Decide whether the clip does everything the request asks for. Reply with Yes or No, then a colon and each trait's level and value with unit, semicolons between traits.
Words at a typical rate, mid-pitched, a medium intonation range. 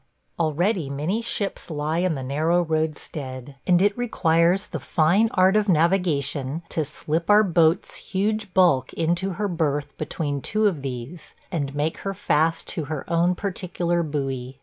Yes: average, 155 wpm; medium, 165 Hz; average, 4.1 semitones